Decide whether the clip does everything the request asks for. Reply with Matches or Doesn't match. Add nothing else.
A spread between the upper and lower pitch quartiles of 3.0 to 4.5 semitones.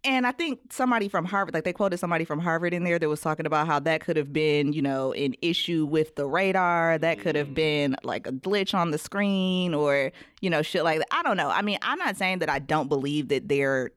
Matches